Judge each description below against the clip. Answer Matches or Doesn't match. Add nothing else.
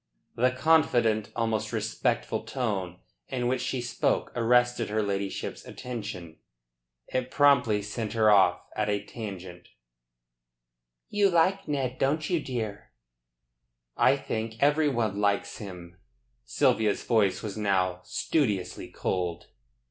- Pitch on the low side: Matches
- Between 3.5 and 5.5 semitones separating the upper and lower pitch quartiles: Matches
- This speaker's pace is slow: Matches